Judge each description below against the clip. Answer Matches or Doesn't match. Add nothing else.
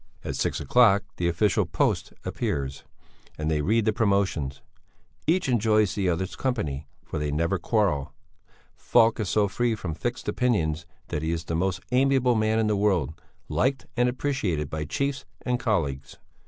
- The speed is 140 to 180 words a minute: Matches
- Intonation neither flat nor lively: Doesn't match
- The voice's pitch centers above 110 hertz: Doesn't match